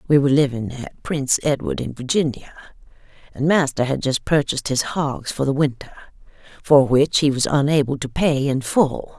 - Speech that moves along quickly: No, average, 175 wpm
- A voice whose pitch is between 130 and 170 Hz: Yes, medium, 140 Hz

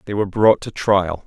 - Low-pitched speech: Yes, low, 100 Hz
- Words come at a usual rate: No, fast, 235 wpm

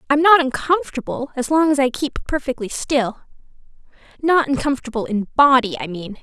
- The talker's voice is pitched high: Yes, very high, 270 Hz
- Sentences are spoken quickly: No, average, 155 wpm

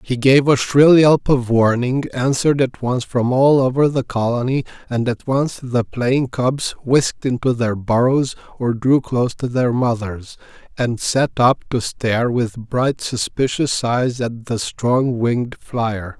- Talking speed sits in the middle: Yes, average, 165 wpm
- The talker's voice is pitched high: No, low, 125 Hz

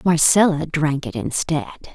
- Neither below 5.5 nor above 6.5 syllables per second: No, 4.5 syllables/s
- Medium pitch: Yes, medium, 155 Hz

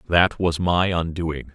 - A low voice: Yes, very low, 85 Hz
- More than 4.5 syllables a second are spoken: No, 3.6 syllables/s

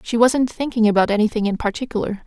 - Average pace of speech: Yes, average, 185 wpm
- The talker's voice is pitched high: Yes, high, 225 Hz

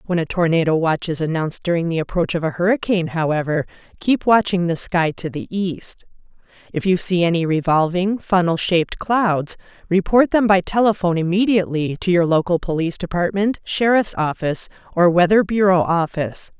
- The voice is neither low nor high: Yes, medium, 175 Hz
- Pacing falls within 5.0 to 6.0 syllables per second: No, 4.2 syllables/s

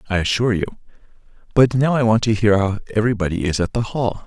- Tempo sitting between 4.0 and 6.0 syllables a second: No, 7.0 syllables/s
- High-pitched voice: No, low, 110 Hz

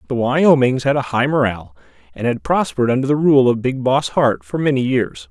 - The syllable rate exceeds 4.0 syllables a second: Yes, 5.5 syllables/s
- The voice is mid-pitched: No, low, 125 Hz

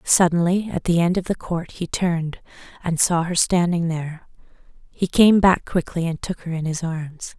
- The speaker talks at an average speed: Yes, average, 195 wpm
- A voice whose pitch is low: No, medium, 170 Hz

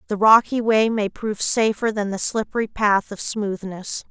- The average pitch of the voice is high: Yes, high, 210 Hz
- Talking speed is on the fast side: No, average, 175 wpm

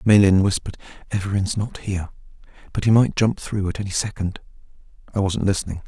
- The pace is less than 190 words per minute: Yes, average, 165 wpm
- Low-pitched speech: Yes, low, 100 Hz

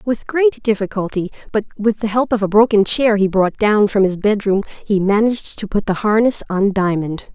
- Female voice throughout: Yes, female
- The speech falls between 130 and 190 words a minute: No, fast, 205 wpm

